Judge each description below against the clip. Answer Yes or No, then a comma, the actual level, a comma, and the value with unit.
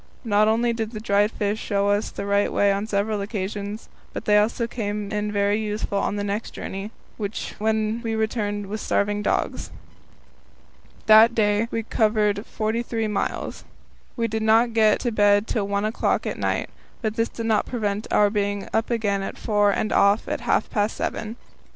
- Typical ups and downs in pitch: No, narrow, 1.5 semitones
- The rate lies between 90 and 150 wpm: No, average, 180 wpm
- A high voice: Yes, high, 210 Hz